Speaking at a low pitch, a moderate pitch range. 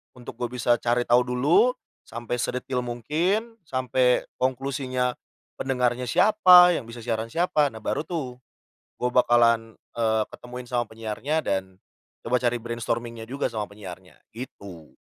No: low, 125 Hz; narrow, 2.2 semitones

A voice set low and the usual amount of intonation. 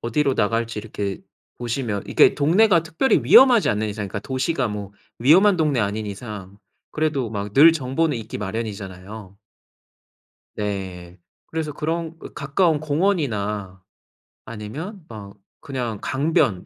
No: low, 115 Hz; wide, 7.2 semitones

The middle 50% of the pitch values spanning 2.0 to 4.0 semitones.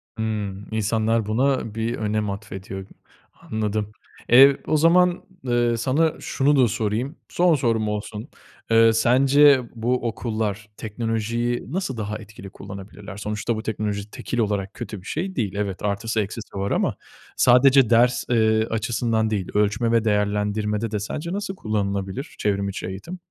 Yes: average, 2.8 semitones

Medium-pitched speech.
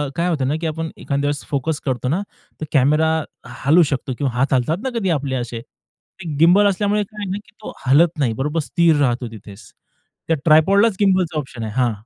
Yes: medium, 150 Hz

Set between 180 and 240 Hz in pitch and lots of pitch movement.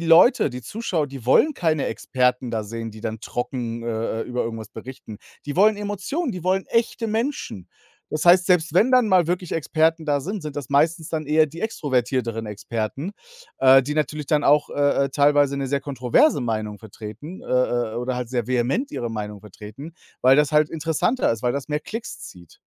No: medium, 140 Hz; wide, 5.9 semitones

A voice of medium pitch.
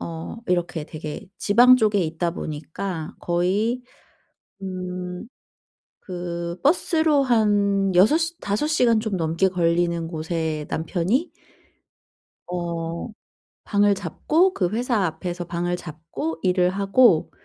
Yes: medium, 180 Hz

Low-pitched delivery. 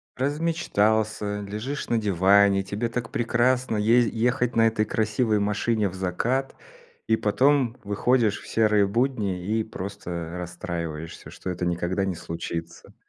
Yes: low, 105 Hz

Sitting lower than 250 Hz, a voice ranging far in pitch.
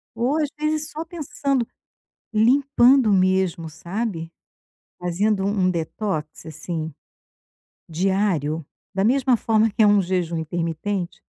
Yes: high, 195 Hz; wide, 6.0 semitones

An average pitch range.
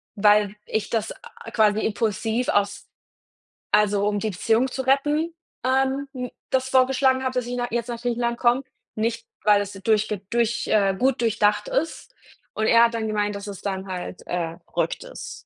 Yes: average, 3.6 semitones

